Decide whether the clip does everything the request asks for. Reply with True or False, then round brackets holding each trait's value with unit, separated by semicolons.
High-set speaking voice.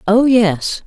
True (205 Hz)